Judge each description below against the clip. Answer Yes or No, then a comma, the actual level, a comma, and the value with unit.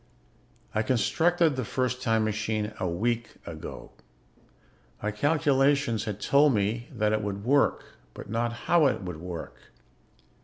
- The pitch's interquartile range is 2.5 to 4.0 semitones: No, average, 4.4 semitones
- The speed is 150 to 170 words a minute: No, average, 140 wpm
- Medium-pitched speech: No, low, 115 Hz